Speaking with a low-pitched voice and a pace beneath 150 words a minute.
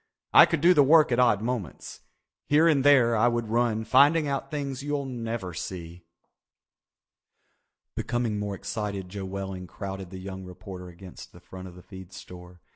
No: low, 105 Hz; average, 170 wpm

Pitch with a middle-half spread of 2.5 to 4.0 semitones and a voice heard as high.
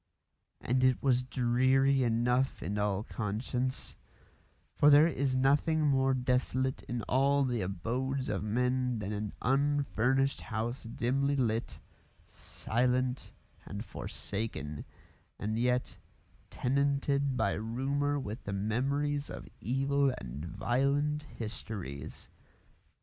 No: average, 3.6 semitones; low, 125 Hz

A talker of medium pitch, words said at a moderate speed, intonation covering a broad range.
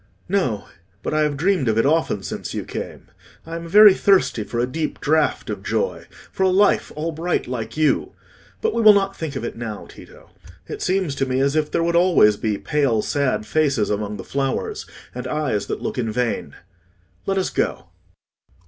Yes: medium, 150 Hz; average, 195 wpm; wide, 6.7 semitones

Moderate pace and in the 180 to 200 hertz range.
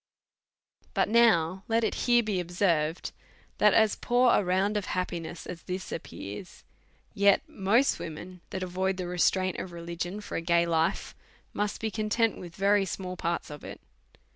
Yes: average, 165 wpm; medium, 185 Hz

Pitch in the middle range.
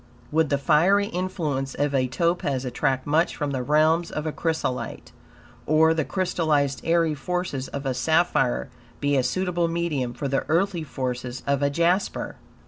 Yes: medium, 150 Hz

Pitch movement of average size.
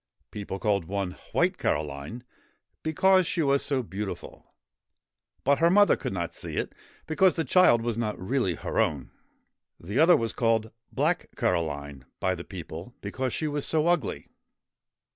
No: wide, 8.7 semitones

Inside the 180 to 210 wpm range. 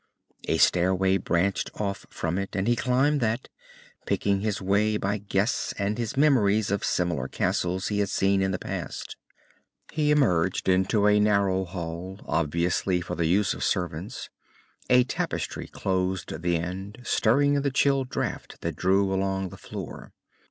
No: average, 160 wpm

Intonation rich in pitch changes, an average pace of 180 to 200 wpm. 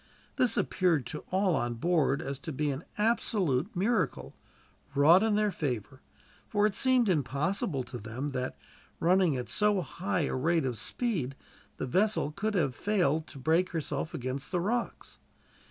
No: wide, 6.8 semitones; average, 155 wpm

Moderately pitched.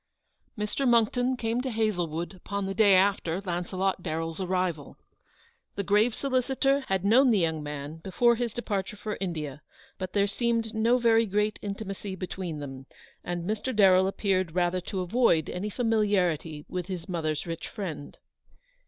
No: high, 195 Hz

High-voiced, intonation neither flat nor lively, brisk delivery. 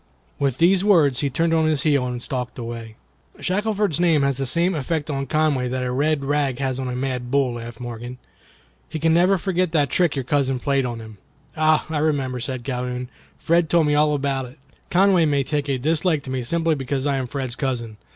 No: medium, 140 Hz; average, 3.9 semitones; fast, 215 wpm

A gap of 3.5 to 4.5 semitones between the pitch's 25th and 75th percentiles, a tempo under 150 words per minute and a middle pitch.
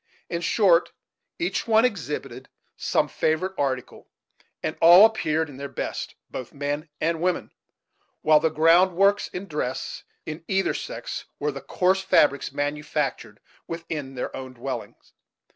Yes: average, 4.2 semitones; average, 140 wpm; medium, 160 Hz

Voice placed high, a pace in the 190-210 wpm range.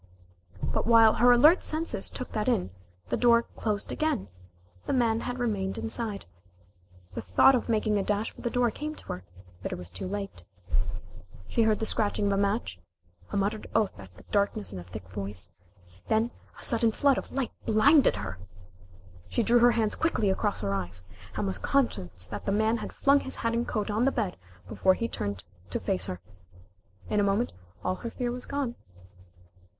Yes: high, 215 Hz; average, 195 wpm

